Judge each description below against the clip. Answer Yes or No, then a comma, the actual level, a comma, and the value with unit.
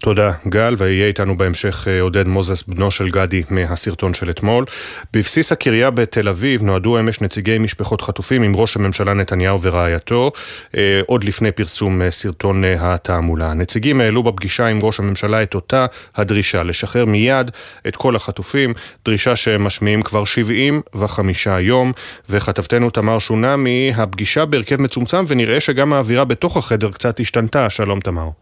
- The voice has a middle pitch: No, low, 105 Hz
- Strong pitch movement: No, average, 3.7 semitones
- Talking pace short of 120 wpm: No, average, 140 wpm